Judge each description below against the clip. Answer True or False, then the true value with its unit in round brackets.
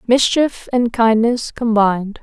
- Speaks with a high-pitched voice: True (230 Hz)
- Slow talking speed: True (110 wpm)